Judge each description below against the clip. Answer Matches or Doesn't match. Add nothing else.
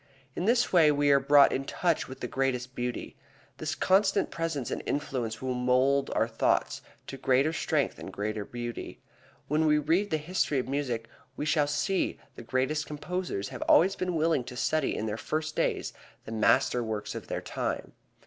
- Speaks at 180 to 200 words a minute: Matches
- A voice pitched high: Doesn't match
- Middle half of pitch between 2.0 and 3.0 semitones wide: Doesn't match